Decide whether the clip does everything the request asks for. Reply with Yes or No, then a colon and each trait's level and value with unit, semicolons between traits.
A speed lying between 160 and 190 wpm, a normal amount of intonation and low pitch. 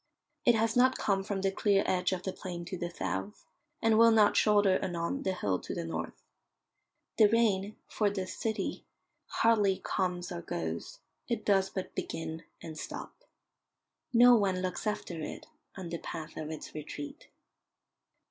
No: average, 165 wpm; average, 4.0 semitones; high, 190 Hz